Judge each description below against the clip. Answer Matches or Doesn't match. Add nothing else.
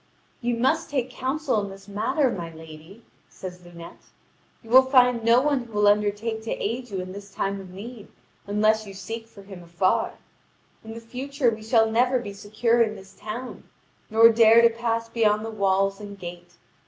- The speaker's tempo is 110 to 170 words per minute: Doesn't match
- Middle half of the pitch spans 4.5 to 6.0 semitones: Doesn't match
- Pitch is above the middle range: Matches